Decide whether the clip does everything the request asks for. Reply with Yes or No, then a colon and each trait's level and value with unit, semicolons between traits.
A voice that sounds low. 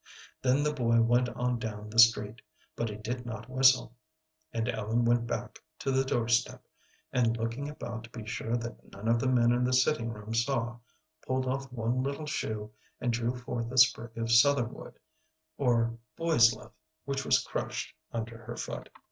Yes: low, 120 Hz